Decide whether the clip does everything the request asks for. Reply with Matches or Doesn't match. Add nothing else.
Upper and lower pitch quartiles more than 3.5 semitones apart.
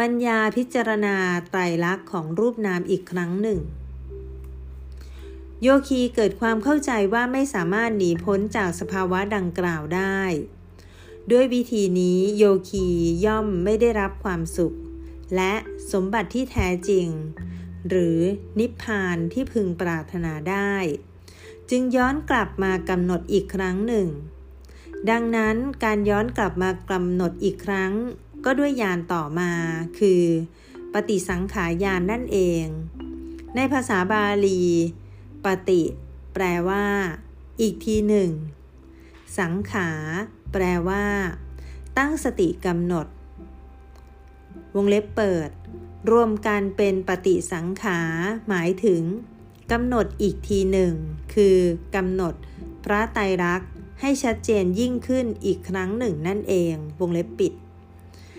Matches